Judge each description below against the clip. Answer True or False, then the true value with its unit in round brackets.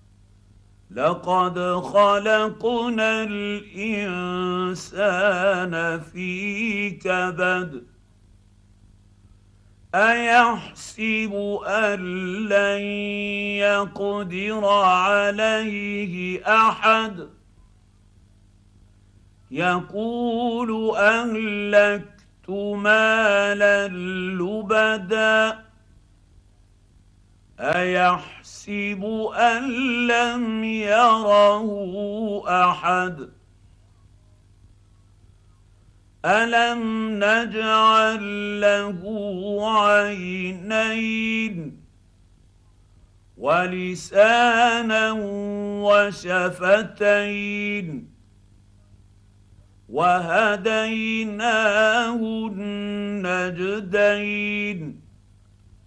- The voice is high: True (200 Hz)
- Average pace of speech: False (30 wpm)